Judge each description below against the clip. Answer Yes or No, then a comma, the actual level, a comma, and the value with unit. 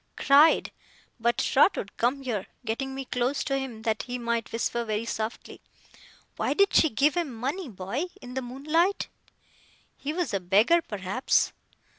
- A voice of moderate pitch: No, very high, 250 Hz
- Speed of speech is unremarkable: Yes, average, 155 wpm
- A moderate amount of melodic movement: Yes, average, 4.1 semitones